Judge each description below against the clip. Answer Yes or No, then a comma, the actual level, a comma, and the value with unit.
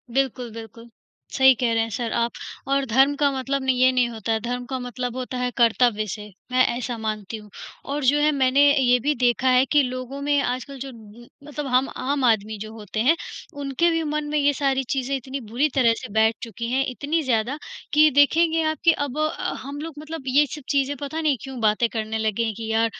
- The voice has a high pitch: Yes, very high, 255 Hz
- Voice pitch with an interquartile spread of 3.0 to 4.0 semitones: Yes, average, 3.6 semitones